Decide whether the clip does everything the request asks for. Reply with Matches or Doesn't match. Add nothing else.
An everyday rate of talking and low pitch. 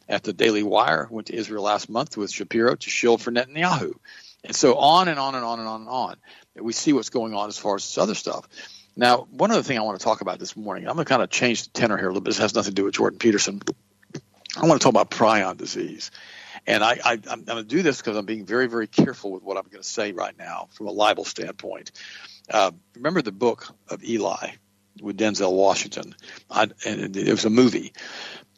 Doesn't match